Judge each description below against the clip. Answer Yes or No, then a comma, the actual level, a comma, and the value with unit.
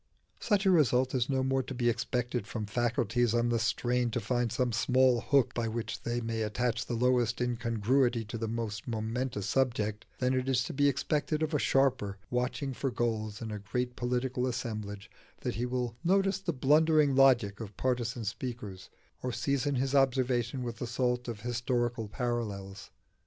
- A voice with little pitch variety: Yes, narrow, 2.3 semitones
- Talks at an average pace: Yes, average, 180 wpm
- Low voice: Yes, low, 120 Hz